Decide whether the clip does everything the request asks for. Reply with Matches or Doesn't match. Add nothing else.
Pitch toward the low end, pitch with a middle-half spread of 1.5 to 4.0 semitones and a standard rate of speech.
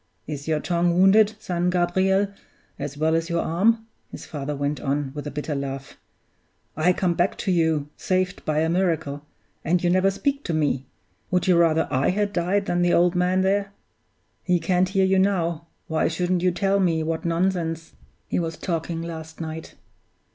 Doesn't match